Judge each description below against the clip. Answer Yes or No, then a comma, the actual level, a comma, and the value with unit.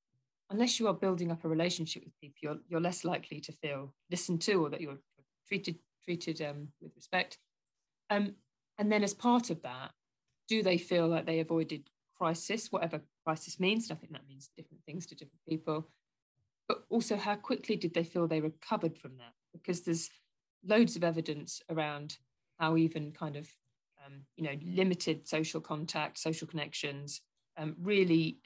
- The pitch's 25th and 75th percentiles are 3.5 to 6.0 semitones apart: No, average, 3.1 semitones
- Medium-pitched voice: Yes, medium, 165 Hz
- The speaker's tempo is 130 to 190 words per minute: Yes, average, 175 wpm